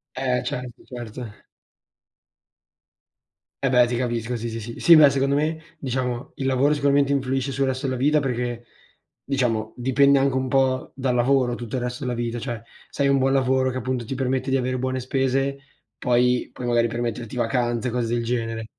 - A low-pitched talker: Yes, low, 125 Hz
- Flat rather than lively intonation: Yes, narrow, 2.0 semitones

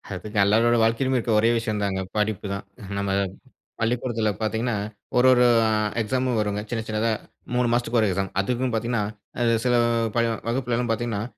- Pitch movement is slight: Yes, narrow, 2.3 semitones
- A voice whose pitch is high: No, low, 115 Hz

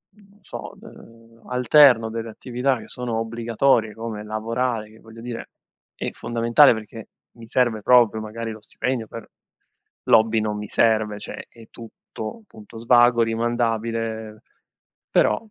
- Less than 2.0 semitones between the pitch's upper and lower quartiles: Yes, narrow, 1.4 semitones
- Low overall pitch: Yes, low, 115 Hz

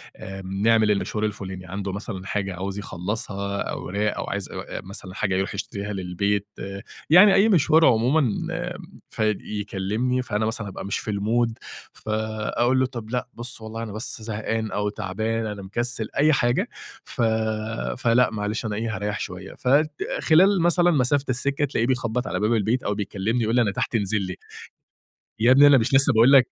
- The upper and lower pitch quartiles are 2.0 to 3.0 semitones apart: No, average, 3.6 semitones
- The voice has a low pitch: Yes, low, 110 Hz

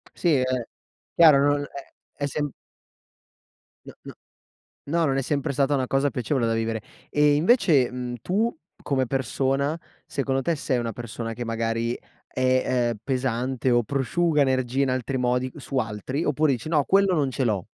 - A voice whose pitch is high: No, low, 135 Hz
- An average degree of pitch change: Yes, average, 3.0 semitones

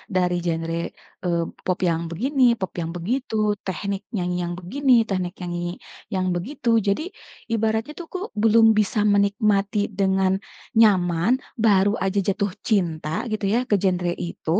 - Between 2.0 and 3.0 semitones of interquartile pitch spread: No, average, 3.6 semitones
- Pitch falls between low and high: No, high, 195 Hz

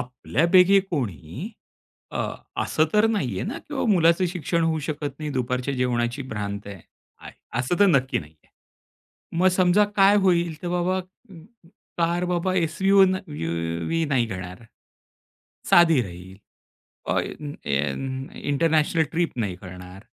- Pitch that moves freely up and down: Yes, wide, 6.9 semitones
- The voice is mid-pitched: Yes, medium, 155 Hz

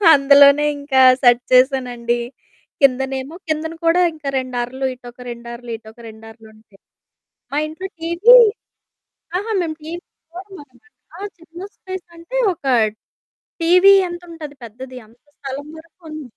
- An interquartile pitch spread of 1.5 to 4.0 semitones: No, average, 5.1 semitones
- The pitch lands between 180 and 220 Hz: No, very high, 280 Hz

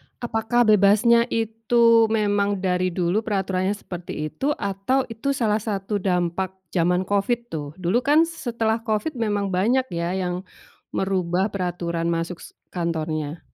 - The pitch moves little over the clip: No, average, 4.0 semitones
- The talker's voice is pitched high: Yes, high, 200 Hz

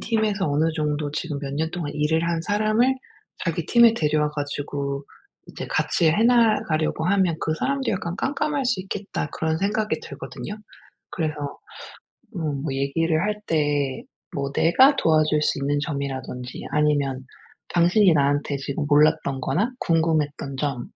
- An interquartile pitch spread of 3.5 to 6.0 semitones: Yes, average, 5.2 semitones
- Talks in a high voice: No, medium, 155 Hz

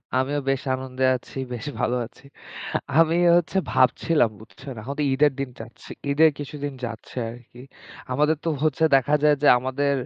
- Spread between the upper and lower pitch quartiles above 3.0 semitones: No, average, 2.7 semitones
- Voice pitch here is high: No, low, 135 Hz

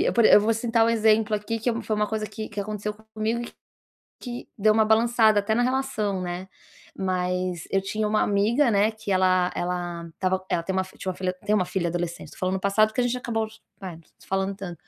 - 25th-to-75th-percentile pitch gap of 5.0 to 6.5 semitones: No, average, 3.0 semitones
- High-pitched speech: Yes, high, 210 Hz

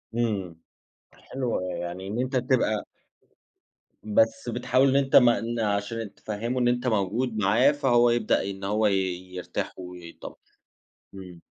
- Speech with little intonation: No, average, 3.8 semitones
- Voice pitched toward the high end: No, low, 110 Hz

